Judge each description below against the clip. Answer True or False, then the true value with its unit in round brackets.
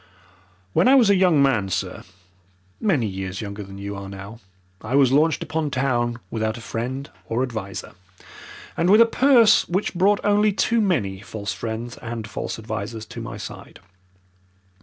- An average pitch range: False (8.9 semitones)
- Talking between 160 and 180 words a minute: True (165 wpm)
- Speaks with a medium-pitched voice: False (120 Hz)